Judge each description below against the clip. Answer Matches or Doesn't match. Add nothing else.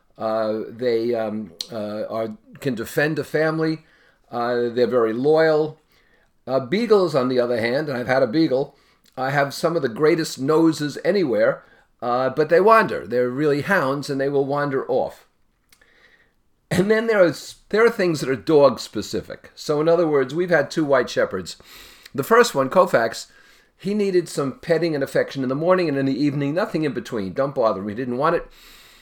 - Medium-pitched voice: Matches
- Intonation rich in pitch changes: Doesn't match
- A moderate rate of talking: Matches